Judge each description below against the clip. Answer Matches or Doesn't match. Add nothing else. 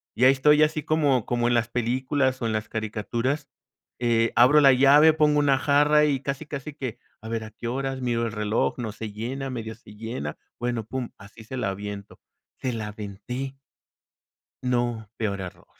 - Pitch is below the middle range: Matches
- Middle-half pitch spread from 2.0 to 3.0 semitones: Doesn't match